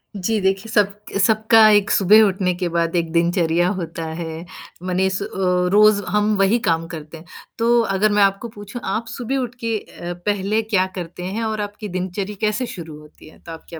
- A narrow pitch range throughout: No, average, 3.6 semitones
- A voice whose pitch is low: No, high, 195 Hz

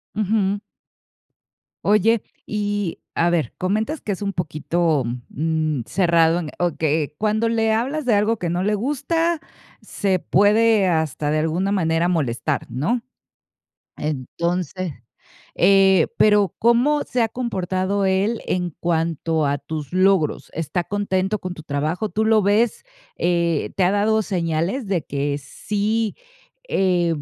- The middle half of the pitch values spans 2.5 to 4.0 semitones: No, average, 4.5 semitones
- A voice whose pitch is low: No, medium, 185 Hz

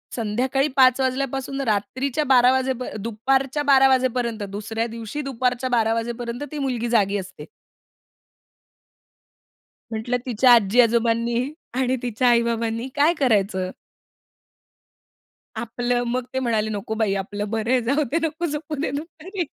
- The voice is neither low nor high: No, high, 245 Hz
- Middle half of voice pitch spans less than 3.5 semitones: Yes, average, 2.9 semitones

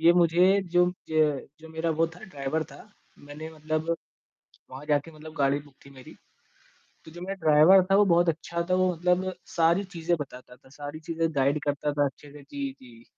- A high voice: No, medium, 160 Hz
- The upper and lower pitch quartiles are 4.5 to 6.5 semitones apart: No, average, 3.2 semitones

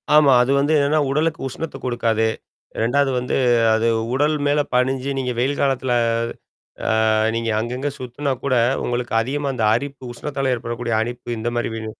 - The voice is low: Yes, low, 130 Hz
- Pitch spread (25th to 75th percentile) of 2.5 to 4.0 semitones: Yes, average, 2.9 semitones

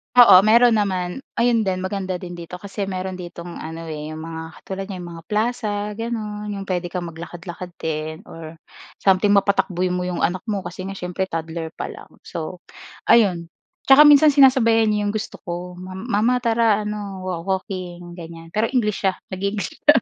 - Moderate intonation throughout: Yes, average, 3.3 semitones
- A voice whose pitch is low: No, medium, 185 Hz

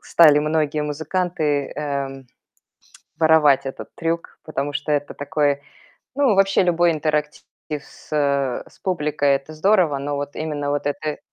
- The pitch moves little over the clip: Yes, narrow, 2.0 semitones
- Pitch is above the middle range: No, medium, 150 Hz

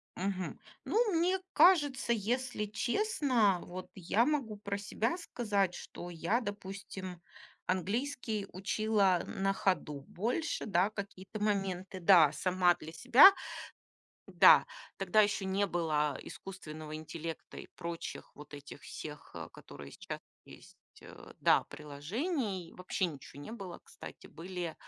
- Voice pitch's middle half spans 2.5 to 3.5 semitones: No, average, 4.3 semitones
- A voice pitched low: No, high, 195 Hz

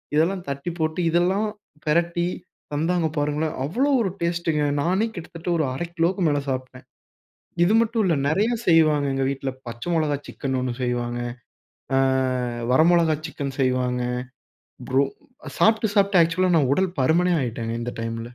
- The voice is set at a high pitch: No, medium, 160 Hz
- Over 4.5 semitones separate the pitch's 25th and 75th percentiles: Yes, average, 4.9 semitones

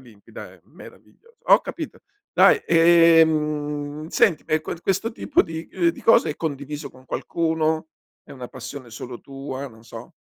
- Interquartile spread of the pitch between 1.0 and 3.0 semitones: No, average, 3.4 semitones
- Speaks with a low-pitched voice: No, medium, 150 Hz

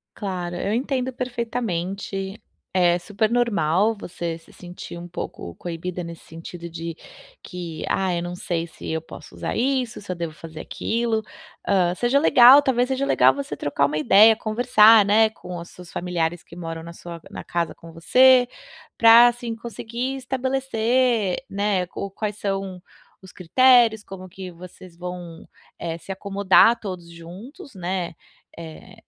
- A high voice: Yes, high, 195 Hz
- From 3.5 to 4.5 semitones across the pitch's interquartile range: No, average, 5.3 semitones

